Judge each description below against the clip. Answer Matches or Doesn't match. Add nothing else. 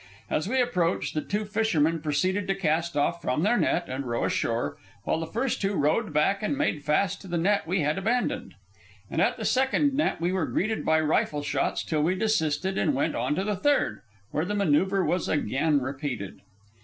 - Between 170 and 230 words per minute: Matches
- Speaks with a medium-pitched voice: Matches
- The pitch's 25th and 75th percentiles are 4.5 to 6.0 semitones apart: Matches